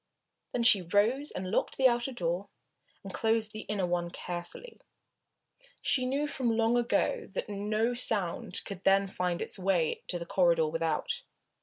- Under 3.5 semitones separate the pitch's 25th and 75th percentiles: No, average, 5.2 semitones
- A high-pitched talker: Yes, high, 205 Hz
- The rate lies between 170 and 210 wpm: No, average, 160 wpm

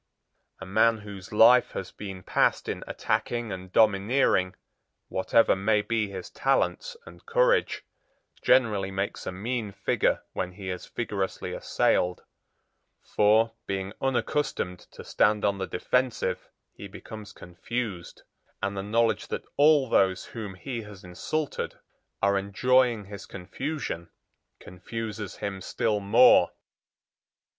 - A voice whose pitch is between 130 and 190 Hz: No, low, 105 Hz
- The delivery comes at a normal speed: No, slow, 125 wpm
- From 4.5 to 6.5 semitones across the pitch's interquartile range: No, average, 3.5 semitones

